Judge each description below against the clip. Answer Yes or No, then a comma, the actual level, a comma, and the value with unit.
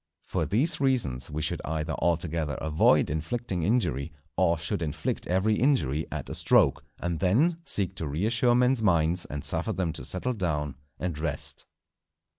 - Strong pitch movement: Yes, wide, 6.0 semitones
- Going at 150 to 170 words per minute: Yes, average, 160 wpm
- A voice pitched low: Yes, very low, 85 Hz